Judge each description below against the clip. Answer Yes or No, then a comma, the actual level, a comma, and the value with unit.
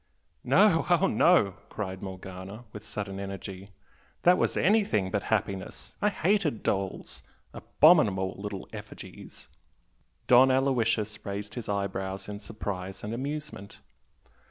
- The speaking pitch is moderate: No, low, 105 Hz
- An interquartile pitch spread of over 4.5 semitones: Yes, wide, 5.6 semitones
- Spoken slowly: Yes, slow, 115 wpm